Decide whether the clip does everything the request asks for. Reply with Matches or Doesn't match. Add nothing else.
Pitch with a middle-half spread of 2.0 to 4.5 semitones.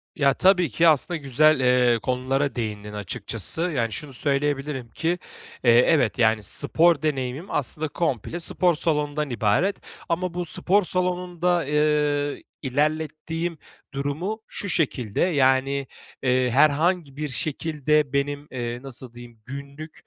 Matches